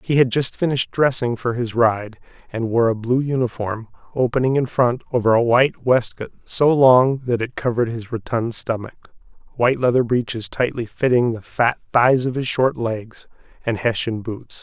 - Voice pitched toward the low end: Yes, low, 120 Hz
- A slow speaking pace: No, average, 175 wpm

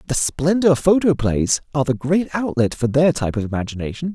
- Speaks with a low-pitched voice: No, medium, 145 Hz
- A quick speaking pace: No, average, 175 wpm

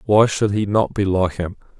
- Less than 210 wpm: No, fast, 235 wpm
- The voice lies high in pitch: No, low, 100 Hz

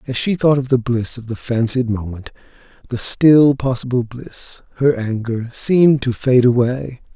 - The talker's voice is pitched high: No, low, 125 Hz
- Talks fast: No, average, 170 wpm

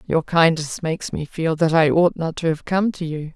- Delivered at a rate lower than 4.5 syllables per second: No, 5.0 syllables/s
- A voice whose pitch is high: No, medium, 165 Hz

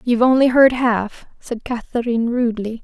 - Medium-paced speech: Yes, average, 150 wpm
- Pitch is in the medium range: No, high, 235 Hz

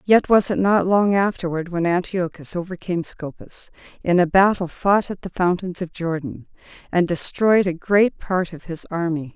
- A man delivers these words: No, female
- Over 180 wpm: No, average, 175 wpm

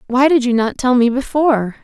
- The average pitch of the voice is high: Yes, very high, 255 Hz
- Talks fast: Yes, fast, 230 wpm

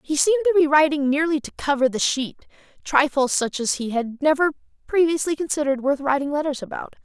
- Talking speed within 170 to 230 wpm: Yes, average, 190 wpm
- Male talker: No, female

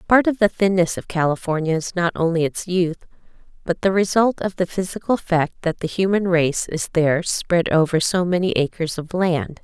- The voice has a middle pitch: Yes, medium, 175 Hz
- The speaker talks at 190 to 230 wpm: Yes, average, 195 wpm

